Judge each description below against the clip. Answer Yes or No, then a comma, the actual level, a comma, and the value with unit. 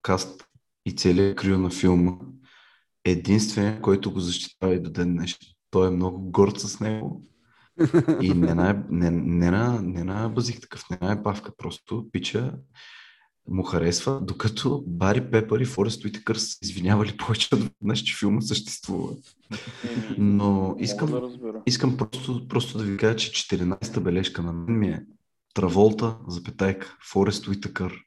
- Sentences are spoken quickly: No, average, 145 wpm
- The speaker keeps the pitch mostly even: No, average, 3.3 semitones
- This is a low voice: Yes, low, 100 Hz